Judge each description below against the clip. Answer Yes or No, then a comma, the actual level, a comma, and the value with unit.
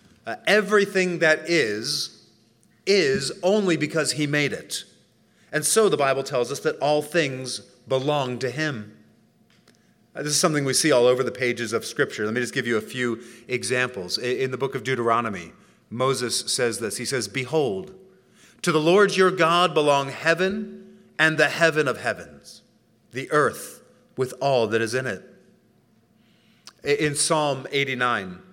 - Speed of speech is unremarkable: Yes, average, 165 wpm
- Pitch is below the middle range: No, medium, 145 Hz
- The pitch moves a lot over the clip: No, average, 4.7 semitones